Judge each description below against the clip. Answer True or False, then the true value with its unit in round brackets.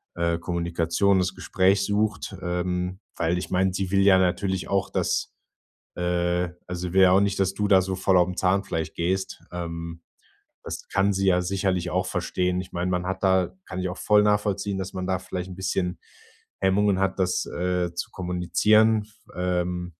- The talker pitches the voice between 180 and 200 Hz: False (90 Hz)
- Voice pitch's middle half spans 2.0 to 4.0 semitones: False (1.5 semitones)